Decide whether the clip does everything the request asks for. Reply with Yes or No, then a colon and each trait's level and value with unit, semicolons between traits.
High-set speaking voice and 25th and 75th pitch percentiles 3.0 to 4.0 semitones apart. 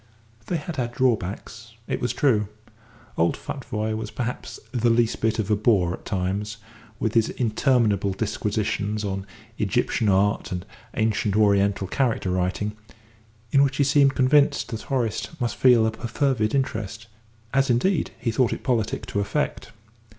No: low, 110 Hz; average, 3.3 semitones